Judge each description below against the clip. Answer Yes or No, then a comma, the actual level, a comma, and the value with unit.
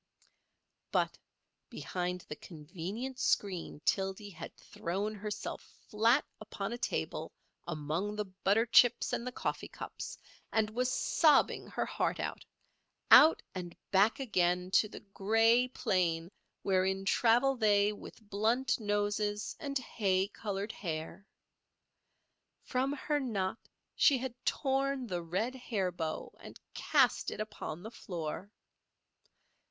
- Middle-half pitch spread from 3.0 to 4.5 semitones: Yes, average, 4.2 semitones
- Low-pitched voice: No, high, 205 Hz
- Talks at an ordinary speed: No, slow, 120 wpm